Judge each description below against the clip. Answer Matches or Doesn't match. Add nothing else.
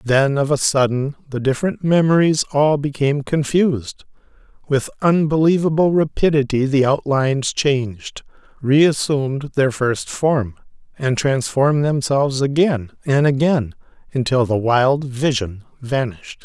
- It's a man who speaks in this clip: Matches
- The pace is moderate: Doesn't match